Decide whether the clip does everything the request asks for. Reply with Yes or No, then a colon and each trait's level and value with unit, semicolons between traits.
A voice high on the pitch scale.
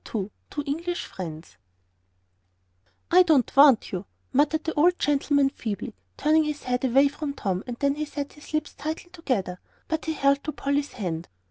Yes: very high, 285 Hz